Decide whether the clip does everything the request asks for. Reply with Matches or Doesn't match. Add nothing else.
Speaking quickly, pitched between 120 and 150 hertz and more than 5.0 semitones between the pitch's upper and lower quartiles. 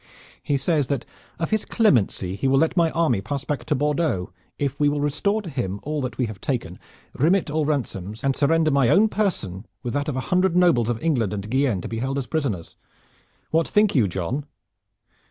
Matches